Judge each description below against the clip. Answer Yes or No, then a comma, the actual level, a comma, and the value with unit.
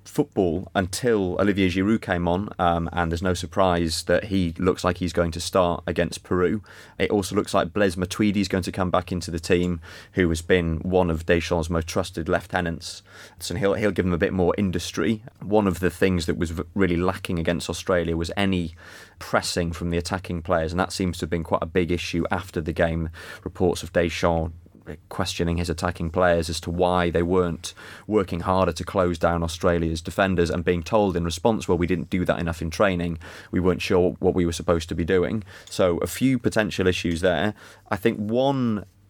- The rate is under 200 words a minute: No, fast, 205 wpm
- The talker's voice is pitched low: Yes, very low, 90 Hz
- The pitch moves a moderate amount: No, narrow, 2.0 semitones